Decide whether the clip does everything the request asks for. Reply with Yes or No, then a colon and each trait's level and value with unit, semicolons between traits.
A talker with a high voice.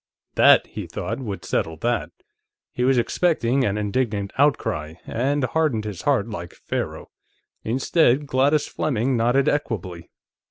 No: low, 120 Hz